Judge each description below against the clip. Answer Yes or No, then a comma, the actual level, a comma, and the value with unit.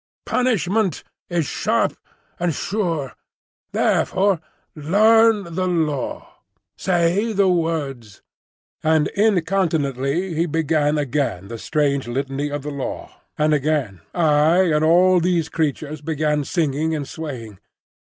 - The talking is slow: Yes, slow, 115 wpm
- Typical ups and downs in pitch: Yes, average, 3.8 semitones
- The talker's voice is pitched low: No, medium, 160 Hz